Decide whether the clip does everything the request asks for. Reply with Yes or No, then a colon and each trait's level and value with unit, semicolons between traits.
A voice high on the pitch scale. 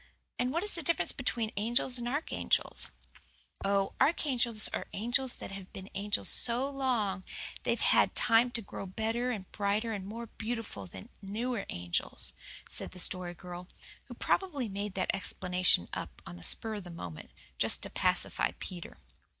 Yes: high, 215 Hz